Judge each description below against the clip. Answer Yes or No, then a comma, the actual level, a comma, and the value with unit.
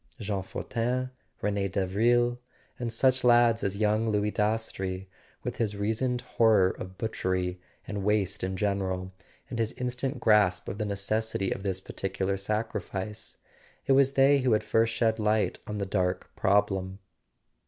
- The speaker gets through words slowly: No, average, 155 wpm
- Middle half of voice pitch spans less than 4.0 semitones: Yes, average, 2.9 semitones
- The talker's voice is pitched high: No, low, 105 Hz